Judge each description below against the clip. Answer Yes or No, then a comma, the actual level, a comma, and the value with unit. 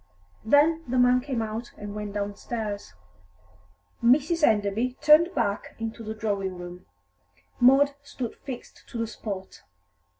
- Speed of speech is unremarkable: No, slow, 130 wpm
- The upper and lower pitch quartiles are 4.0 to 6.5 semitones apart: Yes, average, 4.3 semitones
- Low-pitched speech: No, high, 230 Hz